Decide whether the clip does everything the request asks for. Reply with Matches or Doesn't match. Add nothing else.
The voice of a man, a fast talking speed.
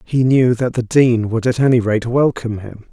Matches